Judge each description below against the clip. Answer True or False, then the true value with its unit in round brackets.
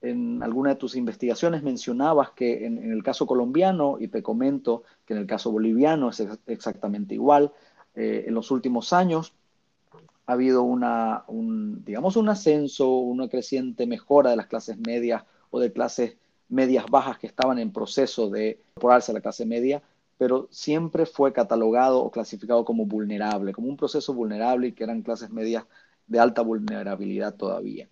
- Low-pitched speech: True (125 Hz)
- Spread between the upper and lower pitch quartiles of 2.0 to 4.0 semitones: True (3.7 semitones)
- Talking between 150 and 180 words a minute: True (170 wpm)